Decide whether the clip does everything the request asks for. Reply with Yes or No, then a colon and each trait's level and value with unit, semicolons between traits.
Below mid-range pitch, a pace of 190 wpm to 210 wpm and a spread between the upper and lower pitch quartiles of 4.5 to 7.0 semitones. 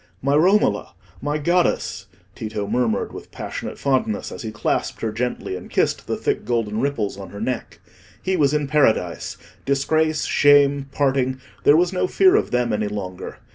No: low, 130 Hz; average, 165 wpm; wide, 5.5 semitones